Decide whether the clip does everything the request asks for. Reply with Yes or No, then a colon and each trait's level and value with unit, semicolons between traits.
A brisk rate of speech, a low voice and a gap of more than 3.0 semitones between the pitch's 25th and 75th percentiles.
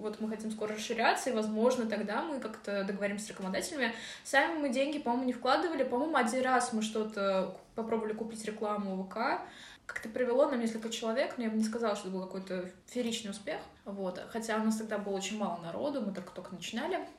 No: fast, 195 wpm; high, 220 Hz; average, 3.6 semitones